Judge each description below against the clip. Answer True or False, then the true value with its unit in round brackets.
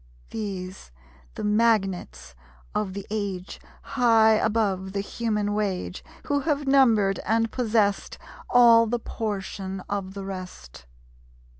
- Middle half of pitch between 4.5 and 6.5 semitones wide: False (3.0 semitones)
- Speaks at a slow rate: True (115 wpm)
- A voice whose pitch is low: False (205 Hz)